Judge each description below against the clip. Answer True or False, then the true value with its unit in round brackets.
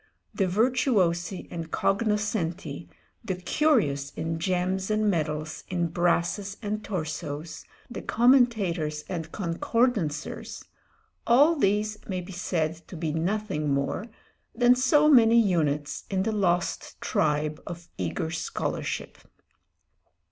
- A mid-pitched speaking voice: True (180 Hz)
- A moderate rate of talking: False (110 wpm)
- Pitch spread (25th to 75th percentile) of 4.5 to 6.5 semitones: True (4.9 semitones)